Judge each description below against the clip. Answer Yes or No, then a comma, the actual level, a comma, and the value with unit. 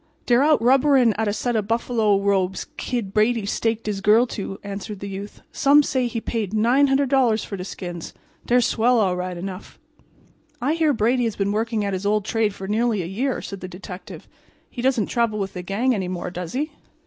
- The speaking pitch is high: Yes, high, 215 Hz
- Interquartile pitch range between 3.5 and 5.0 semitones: Yes, average, 3.8 semitones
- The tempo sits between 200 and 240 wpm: Yes, fast, 205 wpm